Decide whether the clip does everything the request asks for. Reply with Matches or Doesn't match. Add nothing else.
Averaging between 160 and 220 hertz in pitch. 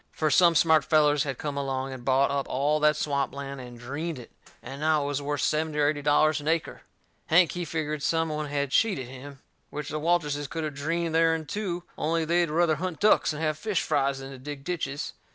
Doesn't match